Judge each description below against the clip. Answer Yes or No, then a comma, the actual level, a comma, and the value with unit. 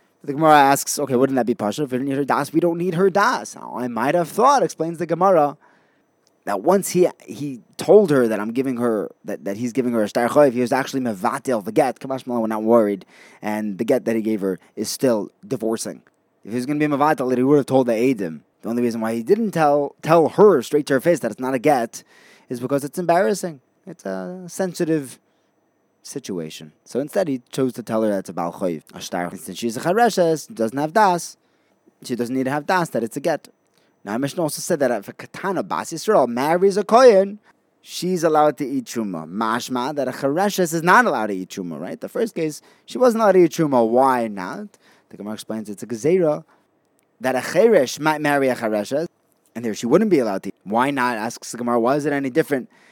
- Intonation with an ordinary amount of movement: No, wide, 6.2 semitones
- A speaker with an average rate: No, fast, 230 wpm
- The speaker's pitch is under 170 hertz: Yes, low, 135 Hz